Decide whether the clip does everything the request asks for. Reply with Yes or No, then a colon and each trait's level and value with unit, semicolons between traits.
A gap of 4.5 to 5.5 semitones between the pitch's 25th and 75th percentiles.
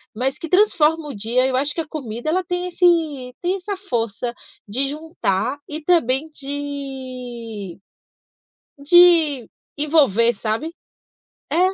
Yes: average, 5.0 semitones